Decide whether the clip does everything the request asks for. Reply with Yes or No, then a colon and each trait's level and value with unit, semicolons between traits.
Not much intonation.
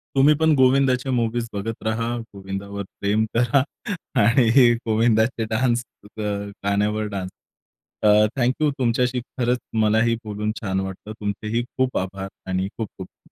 No: average, 3.4 semitones